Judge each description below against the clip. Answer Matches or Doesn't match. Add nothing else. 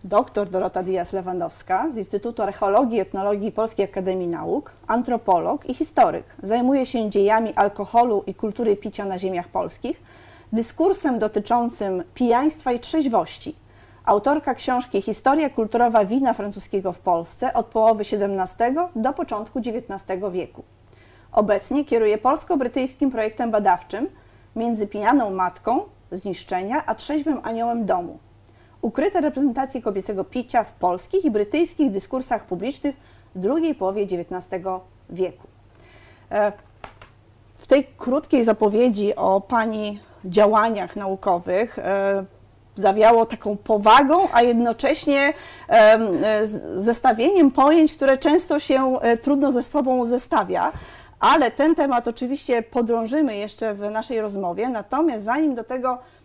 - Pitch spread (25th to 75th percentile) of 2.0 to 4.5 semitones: Doesn't match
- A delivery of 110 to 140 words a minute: Matches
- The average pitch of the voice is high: Matches